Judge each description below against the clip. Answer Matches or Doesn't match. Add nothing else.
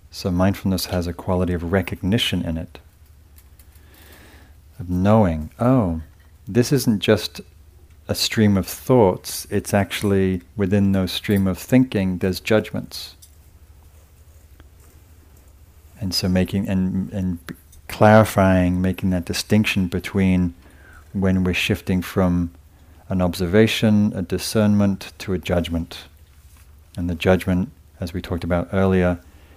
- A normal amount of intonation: Matches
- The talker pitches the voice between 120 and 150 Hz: Doesn't match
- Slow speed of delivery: Matches